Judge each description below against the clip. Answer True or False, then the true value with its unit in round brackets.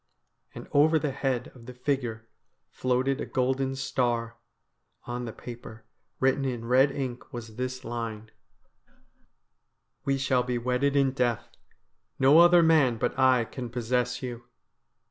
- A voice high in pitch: False (125 Hz)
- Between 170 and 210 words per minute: False (145 wpm)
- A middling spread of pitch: False (2.1 semitones)